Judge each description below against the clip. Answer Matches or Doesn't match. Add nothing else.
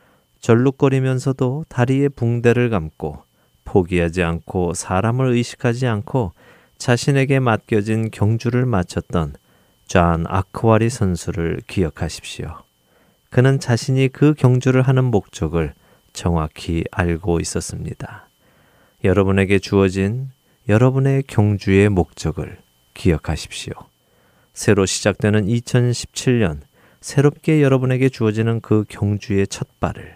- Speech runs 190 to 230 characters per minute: Doesn't match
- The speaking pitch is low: Matches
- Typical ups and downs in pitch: Doesn't match